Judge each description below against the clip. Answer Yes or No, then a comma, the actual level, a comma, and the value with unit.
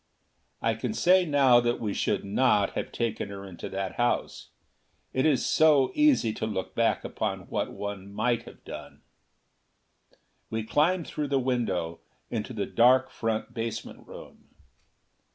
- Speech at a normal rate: Yes, average, 150 wpm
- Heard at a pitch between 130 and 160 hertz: No, low, 115 Hz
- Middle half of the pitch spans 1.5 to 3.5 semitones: No, average, 4.3 semitones